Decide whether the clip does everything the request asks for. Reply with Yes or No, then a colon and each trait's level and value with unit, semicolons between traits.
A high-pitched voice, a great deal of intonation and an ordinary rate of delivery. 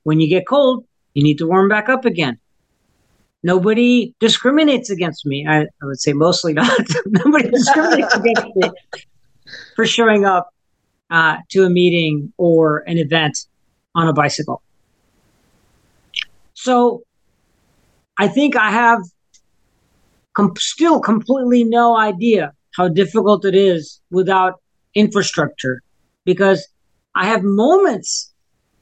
No: high, 195 Hz; wide, 6.3 semitones; slow, 120 wpm